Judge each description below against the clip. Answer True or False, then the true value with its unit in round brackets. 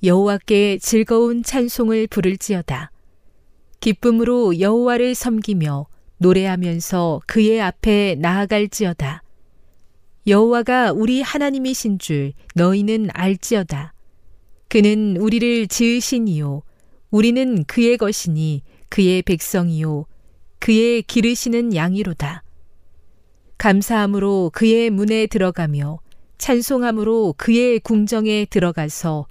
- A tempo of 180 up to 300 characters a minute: True (250 characters per minute)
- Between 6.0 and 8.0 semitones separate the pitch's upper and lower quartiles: True (6.3 semitones)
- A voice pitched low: False (200 Hz)